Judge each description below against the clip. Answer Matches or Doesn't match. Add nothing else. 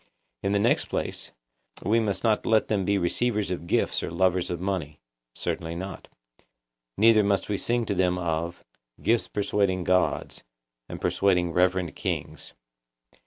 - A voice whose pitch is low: Matches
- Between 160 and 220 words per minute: Doesn't match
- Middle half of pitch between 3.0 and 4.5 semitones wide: Doesn't match